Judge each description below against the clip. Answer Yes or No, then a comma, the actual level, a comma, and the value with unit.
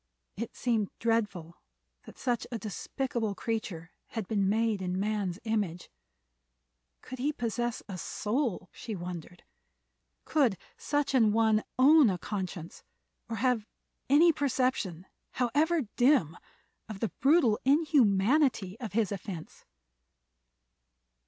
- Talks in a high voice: Yes, high, 225 Hz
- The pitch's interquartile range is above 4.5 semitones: Yes, average, 4.9 semitones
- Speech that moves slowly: Yes, slow, 115 wpm